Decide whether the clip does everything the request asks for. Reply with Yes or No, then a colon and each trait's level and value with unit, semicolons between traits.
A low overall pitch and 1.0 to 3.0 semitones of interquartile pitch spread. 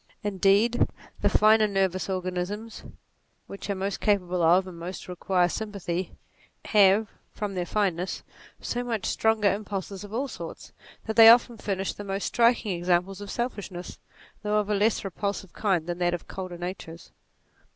No: high, 195 Hz; narrow, 2.6 semitones